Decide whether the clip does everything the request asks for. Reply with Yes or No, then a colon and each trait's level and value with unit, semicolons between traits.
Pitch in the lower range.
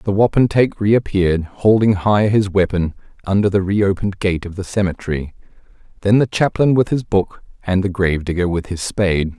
Yes: low, 100 Hz